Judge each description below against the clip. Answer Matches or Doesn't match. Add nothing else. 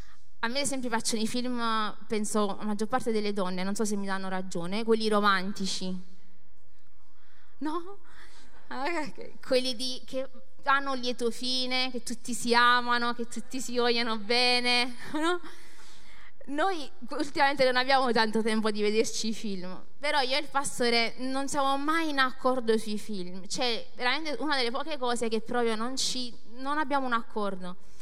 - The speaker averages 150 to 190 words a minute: Matches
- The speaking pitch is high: Matches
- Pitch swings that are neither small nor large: Matches